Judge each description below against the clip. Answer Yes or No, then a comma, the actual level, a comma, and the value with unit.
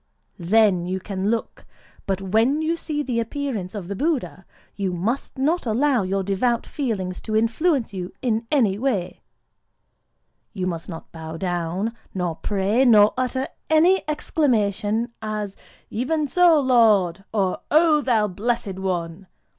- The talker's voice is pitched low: No, high, 215 Hz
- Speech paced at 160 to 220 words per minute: No, average, 140 wpm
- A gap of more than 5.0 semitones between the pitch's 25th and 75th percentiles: Yes, wide, 5.6 semitones